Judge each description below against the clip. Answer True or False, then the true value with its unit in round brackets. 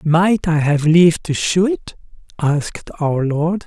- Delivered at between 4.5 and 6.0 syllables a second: False (3.9 syllables/s)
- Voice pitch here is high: False (165 Hz)